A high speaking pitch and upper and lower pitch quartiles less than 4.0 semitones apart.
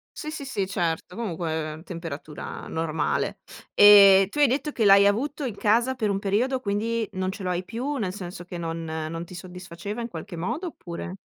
No: high, 195 Hz; average, 5.2 semitones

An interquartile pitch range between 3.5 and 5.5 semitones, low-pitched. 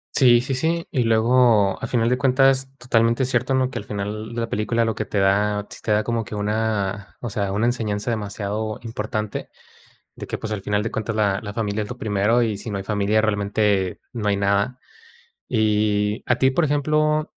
No: average, 2.8 semitones; low, 110 Hz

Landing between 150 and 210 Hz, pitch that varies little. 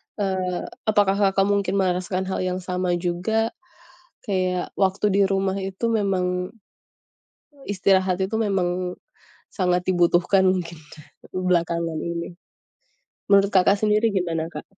Yes: high, 190 Hz; narrow, 1.8 semitones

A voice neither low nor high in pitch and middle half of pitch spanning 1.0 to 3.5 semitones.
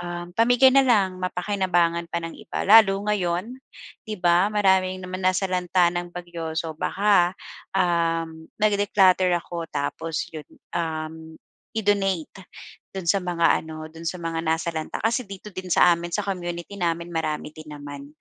Yes: medium, 175 Hz; average, 2.8 semitones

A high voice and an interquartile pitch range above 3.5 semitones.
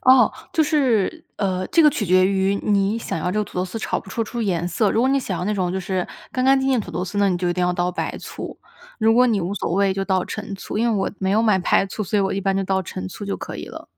No: high, 195 Hz; average, 3.2 semitones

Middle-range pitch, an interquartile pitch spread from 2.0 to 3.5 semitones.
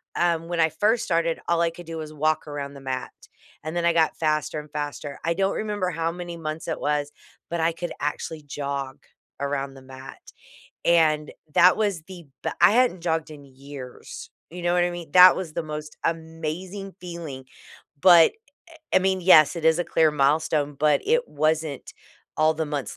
Yes: medium, 160 Hz; average, 2.8 semitones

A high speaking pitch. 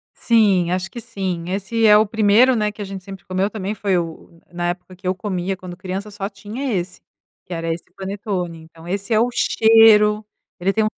Yes: high, 195 Hz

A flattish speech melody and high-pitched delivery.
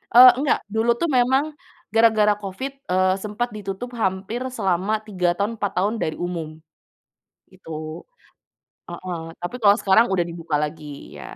No: average, 3.8 semitones; high, 200 Hz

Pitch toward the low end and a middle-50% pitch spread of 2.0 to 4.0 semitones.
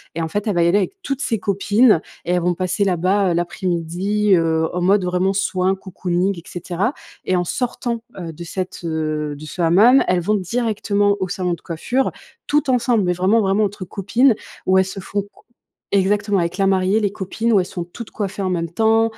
No: high, 190 Hz; average, 2.9 semitones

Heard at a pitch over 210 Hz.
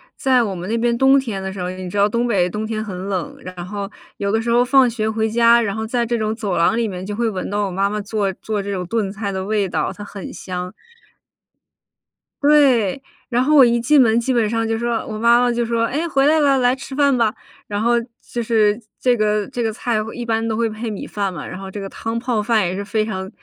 Yes: high, 220 Hz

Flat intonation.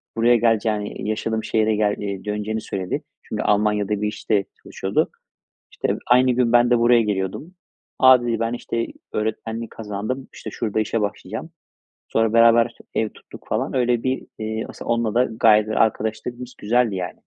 Yes: narrow, 2.1 semitones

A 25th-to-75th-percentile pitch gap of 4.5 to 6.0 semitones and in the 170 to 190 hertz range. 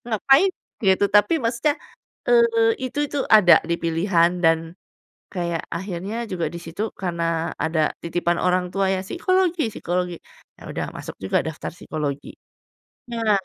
Yes: average, 5.3 semitones; medium, 185 Hz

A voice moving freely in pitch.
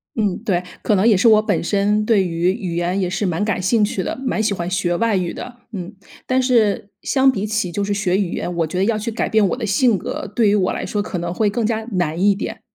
No: average, 3.1 semitones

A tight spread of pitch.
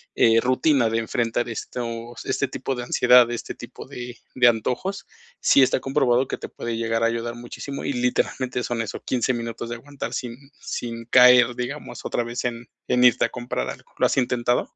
Yes: narrow, 1.3 semitones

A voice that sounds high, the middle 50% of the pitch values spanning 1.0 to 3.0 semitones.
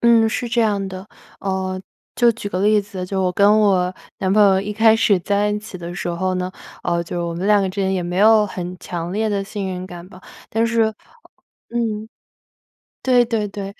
Yes: high, 200 Hz; narrow, 2.6 semitones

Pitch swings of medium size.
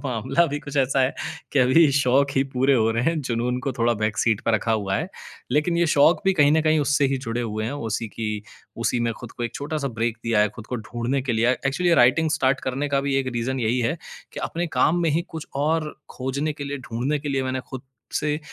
Yes: average, 3.9 semitones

